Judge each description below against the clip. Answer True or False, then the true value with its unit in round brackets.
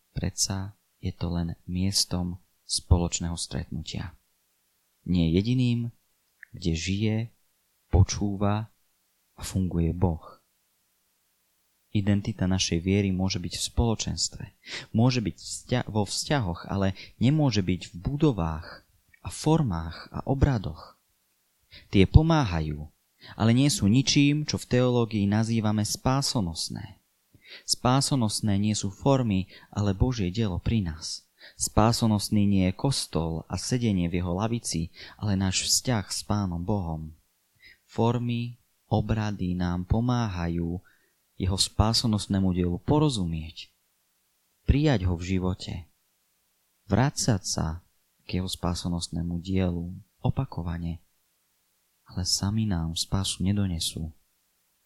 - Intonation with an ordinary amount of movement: True (4.2 semitones)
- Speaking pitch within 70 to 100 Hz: True (95 Hz)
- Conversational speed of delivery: False (105 wpm)